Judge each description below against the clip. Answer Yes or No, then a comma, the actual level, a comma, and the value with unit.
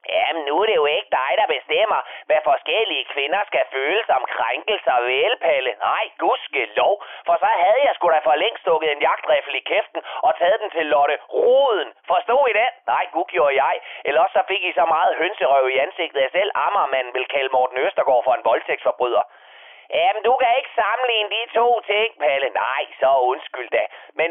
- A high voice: Yes, high, 210 Hz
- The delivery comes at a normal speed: Yes, average, 195 wpm